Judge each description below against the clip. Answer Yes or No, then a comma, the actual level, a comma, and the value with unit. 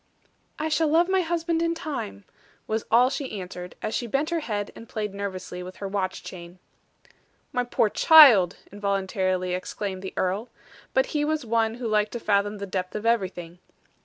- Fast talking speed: No, average, 180 wpm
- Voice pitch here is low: No, high, 210 Hz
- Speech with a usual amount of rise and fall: No, wide, 6.5 semitones